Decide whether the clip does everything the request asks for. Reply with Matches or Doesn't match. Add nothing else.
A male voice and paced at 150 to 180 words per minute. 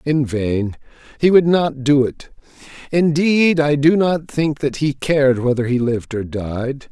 Matches